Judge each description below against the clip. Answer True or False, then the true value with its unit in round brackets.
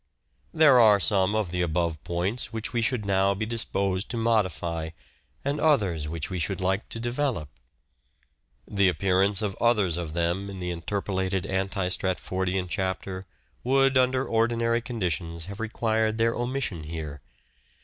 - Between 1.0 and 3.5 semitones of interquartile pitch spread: False (4.2 semitones)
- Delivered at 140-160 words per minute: True (150 wpm)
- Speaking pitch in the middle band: False (95 Hz)